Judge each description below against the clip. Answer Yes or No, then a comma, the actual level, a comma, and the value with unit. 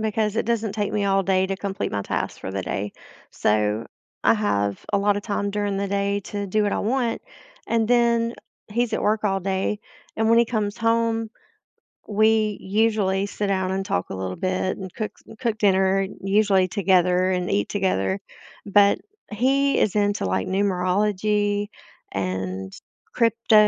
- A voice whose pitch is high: Yes, high, 200 Hz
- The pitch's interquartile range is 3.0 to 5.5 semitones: No, narrow, 2.5 semitones